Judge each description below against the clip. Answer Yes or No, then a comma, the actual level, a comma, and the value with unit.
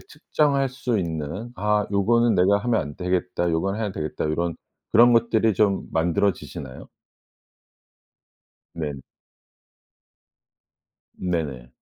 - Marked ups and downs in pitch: Yes, wide, 5.8 semitones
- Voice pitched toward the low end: Yes, very low, 95 Hz